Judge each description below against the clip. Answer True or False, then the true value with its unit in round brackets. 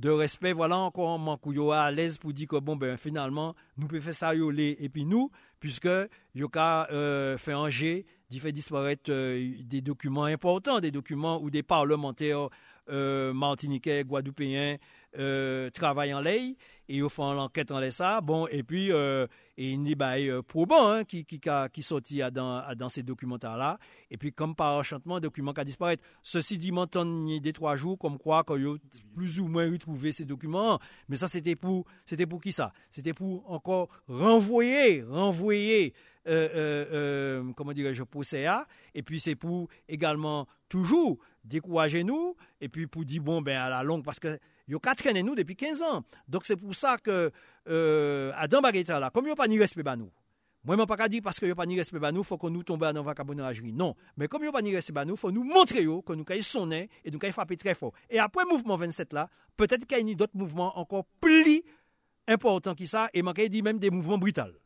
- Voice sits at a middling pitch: True (160 Hz)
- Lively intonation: False (4.5 semitones)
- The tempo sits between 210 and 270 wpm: True (215 wpm)